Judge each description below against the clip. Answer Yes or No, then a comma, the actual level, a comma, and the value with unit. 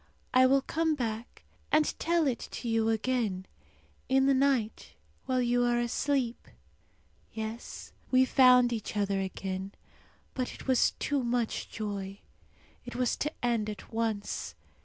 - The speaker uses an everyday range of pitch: Yes, average, 3.1 semitones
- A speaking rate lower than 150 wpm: Yes, average, 140 wpm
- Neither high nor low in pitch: No, high, 240 Hz